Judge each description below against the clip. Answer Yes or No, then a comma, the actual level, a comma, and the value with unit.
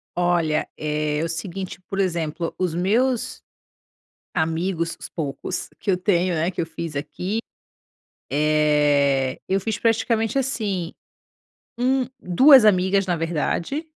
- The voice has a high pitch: No, medium, 175 Hz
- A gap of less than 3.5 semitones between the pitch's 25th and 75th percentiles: No, average, 4.2 semitones